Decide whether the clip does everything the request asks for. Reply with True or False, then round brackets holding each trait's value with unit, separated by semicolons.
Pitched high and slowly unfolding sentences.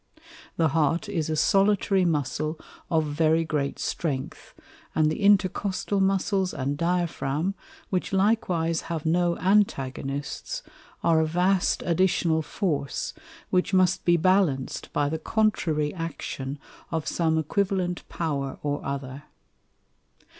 False (165 Hz; 120 wpm)